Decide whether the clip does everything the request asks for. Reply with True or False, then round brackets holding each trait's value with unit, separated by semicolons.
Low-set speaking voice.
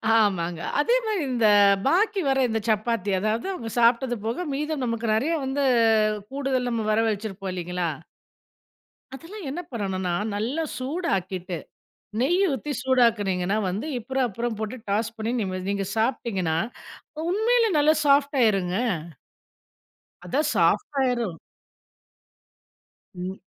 False (230 Hz)